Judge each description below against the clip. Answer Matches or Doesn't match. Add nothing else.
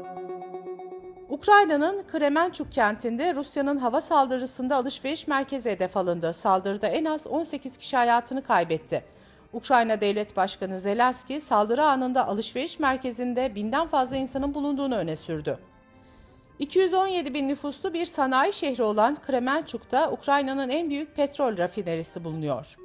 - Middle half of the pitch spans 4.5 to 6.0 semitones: Matches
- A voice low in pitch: Doesn't match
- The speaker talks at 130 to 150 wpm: Doesn't match